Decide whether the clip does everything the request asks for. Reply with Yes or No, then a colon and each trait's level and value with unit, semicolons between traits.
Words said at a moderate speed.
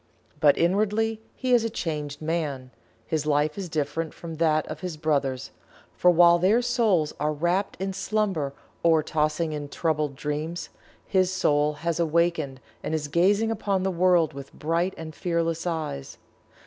Yes: average, 160 wpm